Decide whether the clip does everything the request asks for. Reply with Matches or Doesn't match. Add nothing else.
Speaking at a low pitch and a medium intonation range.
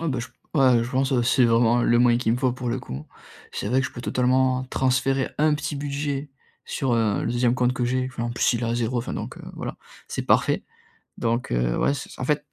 Doesn't match